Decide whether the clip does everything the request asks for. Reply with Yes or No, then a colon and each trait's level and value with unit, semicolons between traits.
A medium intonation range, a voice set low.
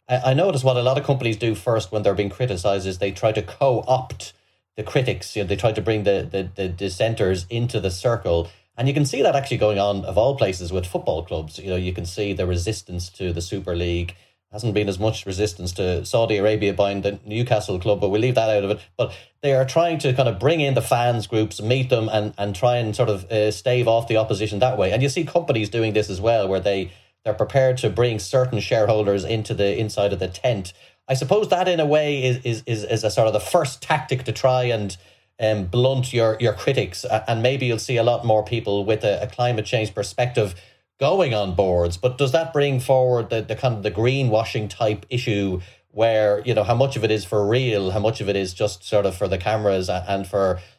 Yes: average, 3.9 semitones; low, 110 Hz